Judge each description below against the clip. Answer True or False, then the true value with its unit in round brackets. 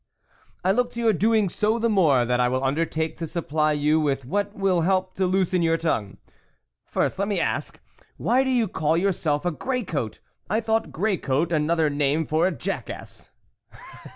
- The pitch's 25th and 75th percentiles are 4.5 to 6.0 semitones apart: True (5.0 semitones)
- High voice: False (170 Hz)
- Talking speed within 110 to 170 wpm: False (195 wpm)